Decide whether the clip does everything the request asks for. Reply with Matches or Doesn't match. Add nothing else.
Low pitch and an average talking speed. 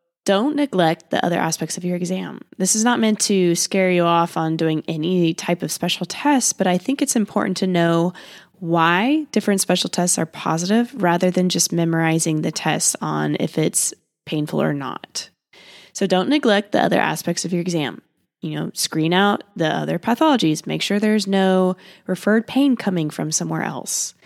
Doesn't match